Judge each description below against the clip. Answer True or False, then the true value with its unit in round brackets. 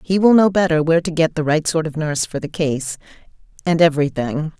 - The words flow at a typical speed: False (210 wpm)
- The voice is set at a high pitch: False (160 Hz)